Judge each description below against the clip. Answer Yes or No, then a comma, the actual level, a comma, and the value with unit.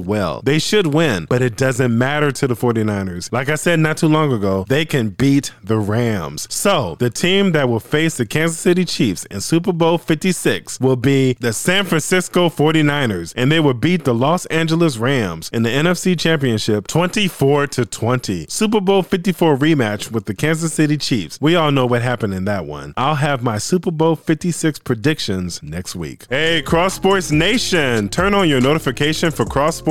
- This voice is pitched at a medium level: Yes, medium, 145 Hz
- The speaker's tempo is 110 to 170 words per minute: No, average, 190 wpm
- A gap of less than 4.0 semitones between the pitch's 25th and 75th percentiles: No, wide, 5.5 semitones